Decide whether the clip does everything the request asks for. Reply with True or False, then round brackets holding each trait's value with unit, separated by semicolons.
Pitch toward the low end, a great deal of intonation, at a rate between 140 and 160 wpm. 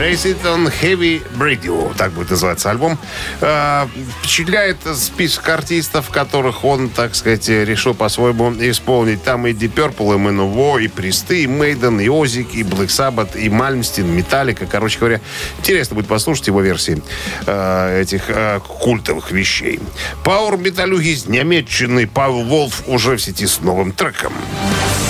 True (120 Hz; 6.1 semitones; 145 wpm)